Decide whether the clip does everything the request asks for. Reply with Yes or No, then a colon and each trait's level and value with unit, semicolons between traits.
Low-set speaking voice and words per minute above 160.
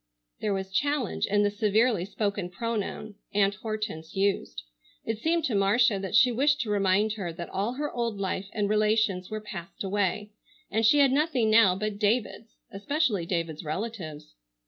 No: high, 210 Hz; average, 170 wpm